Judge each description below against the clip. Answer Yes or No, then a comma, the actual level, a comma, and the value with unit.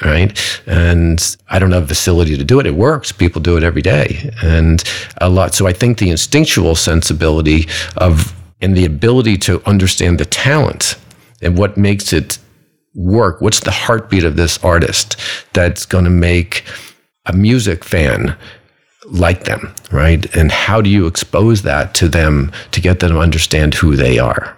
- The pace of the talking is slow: No, average, 170 wpm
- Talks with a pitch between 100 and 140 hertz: No, very low, 90 Hz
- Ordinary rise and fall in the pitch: Yes, average, 3.5 semitones